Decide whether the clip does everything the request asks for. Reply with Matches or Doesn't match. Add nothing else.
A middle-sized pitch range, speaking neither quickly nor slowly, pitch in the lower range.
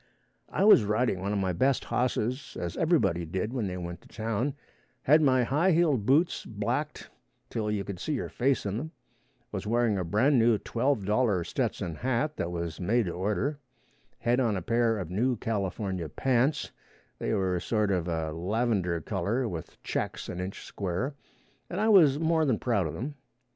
Doesn't match